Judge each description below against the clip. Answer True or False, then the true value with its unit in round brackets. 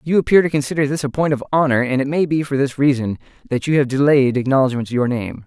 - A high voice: False (140 Hz)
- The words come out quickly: True (255 wpm)